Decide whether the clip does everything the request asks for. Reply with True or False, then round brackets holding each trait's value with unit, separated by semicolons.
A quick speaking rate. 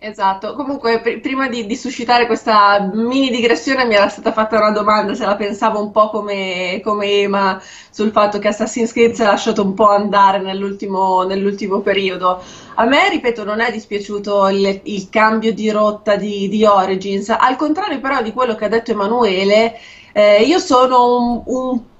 True (180 wpm)